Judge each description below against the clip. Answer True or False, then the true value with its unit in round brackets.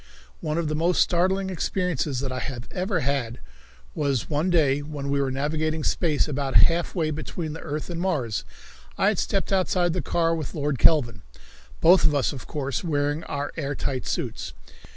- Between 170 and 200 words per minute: True (185 wpm)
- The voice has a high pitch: False (150 Hz)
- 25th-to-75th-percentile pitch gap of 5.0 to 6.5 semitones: False (3.5 semitones)